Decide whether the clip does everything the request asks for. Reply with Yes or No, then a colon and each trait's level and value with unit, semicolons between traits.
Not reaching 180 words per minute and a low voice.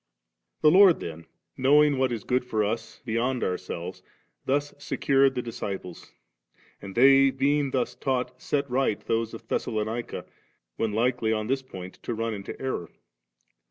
Yes: average, 160 wpm; low, 125 Hz